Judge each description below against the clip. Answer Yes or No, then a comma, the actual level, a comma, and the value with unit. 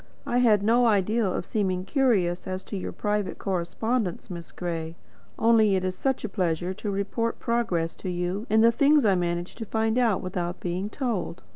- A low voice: No, high, 200 Hz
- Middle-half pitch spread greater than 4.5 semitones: No, average, 4.2 semitones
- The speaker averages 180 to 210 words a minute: Yes, average, 185 wpm